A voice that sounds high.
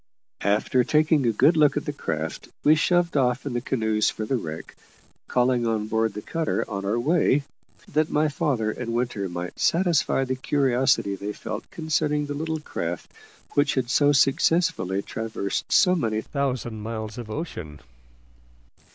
No: low, 125 Hz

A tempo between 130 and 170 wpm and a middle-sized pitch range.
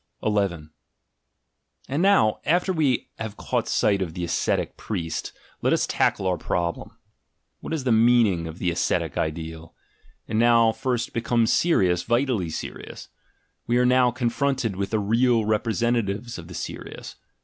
Yes: average, 150 wpm; average, 5.0 semitones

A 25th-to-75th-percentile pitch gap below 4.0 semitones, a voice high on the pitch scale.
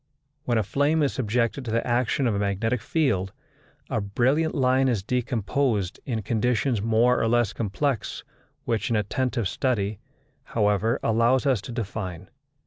No: average, 3.6 semitones; low, 115 Hz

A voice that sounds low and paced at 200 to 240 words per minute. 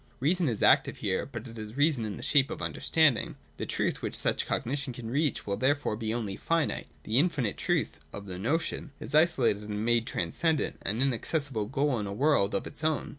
Yes: low, 125 Hz; fast, 205 wpm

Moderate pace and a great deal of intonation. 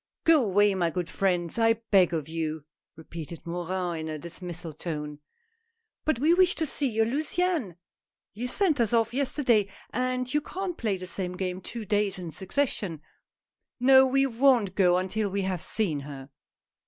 Yes: average, 175 wpm; wide, 6.6 semitones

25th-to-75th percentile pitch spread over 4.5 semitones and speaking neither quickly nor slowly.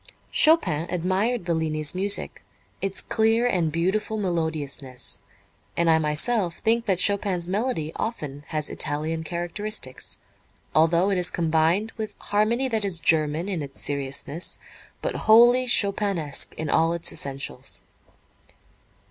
No: average, 5.0 semitones; slow, 120 wpm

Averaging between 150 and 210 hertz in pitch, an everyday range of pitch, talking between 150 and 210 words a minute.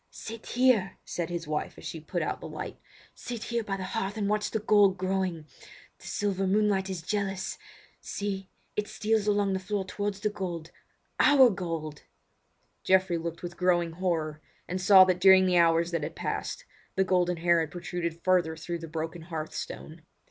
Yes: medium, 185 Hz; average, 3.1 semitones; average, 180 wpm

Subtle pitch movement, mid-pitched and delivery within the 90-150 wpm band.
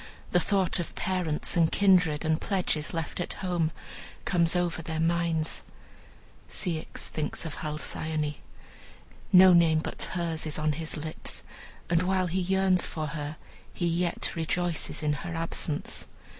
Yes: narrow, 2.1 semitones; medium, 165 Hz; average, 145 wpm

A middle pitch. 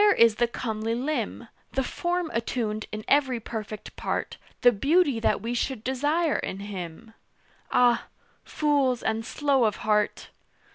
No: high, 240 Hz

